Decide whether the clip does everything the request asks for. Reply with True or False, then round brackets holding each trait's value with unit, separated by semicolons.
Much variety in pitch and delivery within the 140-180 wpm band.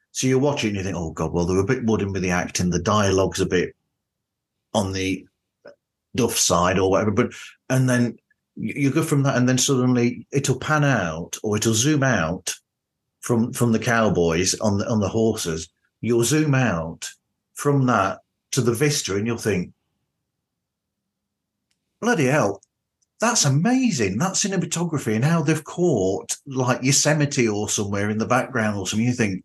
True (5.8 semitones; 170 wpm)